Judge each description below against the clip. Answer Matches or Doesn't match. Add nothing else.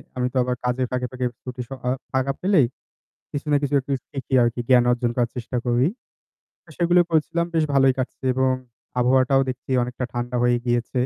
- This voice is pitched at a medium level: Doesn't match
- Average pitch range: Doesn't match